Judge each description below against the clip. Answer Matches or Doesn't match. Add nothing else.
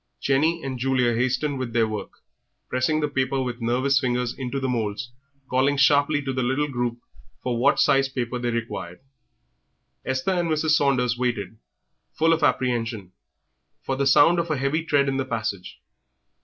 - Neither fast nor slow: Matches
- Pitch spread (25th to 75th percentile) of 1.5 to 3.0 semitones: Matches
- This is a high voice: Doesn't match